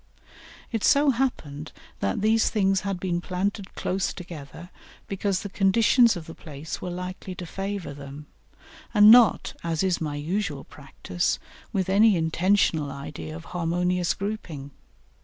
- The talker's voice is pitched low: No, medium, 180 Hz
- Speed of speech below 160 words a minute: Yes, average, 140 wpm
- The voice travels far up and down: No, average, 4.3 semitones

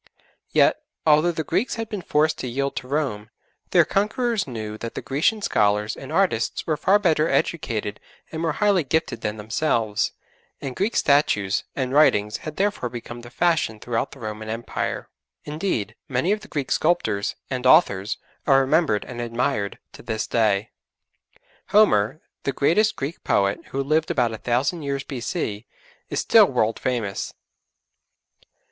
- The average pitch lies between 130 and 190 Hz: Yes, low, 135 Hz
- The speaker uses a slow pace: No, average, 155 wpm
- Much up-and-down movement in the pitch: Yes, wide, 6.5 semitones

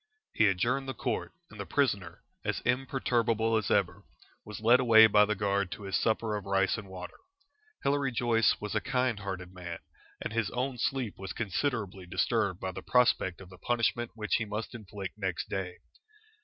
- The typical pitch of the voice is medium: No, low, 105 Hz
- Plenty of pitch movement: No, average, 3.6 semitones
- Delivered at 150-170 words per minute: No, average, 185 wpm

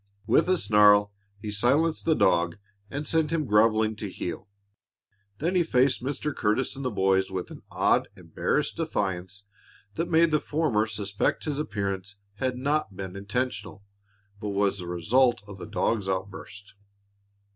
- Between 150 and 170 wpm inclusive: Yes, average, 155 wpm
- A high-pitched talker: No, low, 105 Hz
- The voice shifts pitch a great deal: Yes, wide, 5.7 semitones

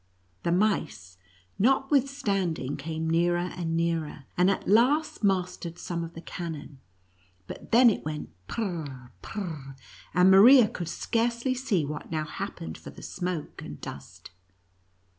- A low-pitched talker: No, medium, 175 Hz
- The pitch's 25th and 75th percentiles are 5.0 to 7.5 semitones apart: Yes, average, 5.3 semitones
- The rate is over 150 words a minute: No, average, 140 wpm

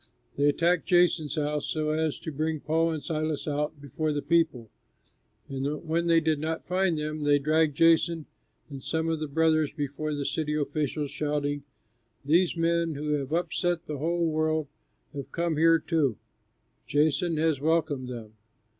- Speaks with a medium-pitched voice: Yes, medium, 155 Hz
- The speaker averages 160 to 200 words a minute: Yes, average, 165 wpm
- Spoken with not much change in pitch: Yes, narrow, 2.0 semitones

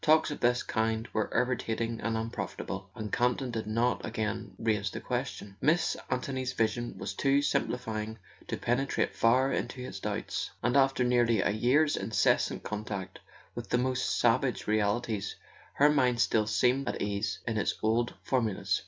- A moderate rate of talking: Yes, average, 160 wpm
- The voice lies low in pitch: Yes, low, 115 Hz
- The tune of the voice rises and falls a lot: No, average, 2.8 semitones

